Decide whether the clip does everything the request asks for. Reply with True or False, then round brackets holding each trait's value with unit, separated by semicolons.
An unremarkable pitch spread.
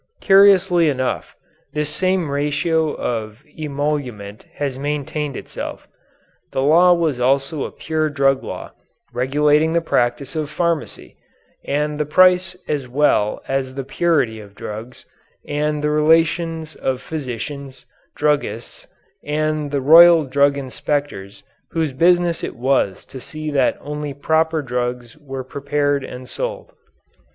True (3.1 semitones)